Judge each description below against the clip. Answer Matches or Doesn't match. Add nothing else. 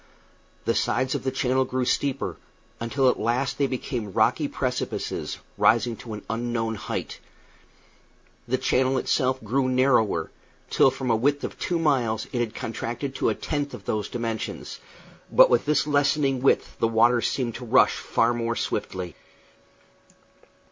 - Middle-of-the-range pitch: Doesn't match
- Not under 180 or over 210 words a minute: Doesn't match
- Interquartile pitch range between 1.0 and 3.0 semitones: Matches